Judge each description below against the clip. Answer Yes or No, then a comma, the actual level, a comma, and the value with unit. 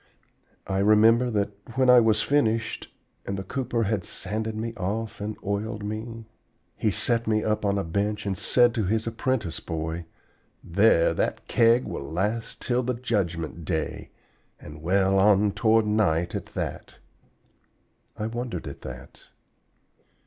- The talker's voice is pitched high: No, low, 105 Hz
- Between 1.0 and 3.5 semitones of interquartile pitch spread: Yes, average, 3.1 semitones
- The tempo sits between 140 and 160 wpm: Yes, average, 150 wpm